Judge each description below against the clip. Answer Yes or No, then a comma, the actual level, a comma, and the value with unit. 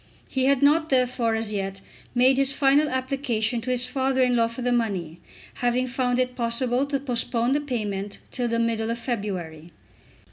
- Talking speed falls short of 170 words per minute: No, average, 180 wpm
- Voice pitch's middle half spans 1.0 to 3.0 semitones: Yes, narrow, 2.6 semitones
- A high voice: Yes, high, 245 Hz